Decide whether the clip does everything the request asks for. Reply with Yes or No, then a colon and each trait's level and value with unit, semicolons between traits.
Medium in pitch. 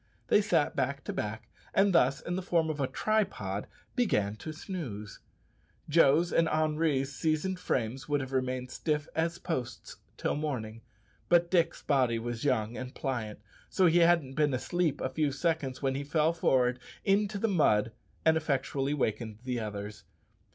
Yes: medium, 145 Hz